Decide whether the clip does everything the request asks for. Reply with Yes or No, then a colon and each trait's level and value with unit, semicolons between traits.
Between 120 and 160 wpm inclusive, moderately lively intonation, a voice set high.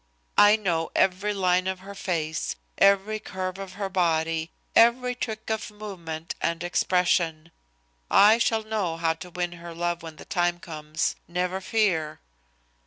No: average, 150 wpm; average, 3.6 semitones; medium, 180 Hz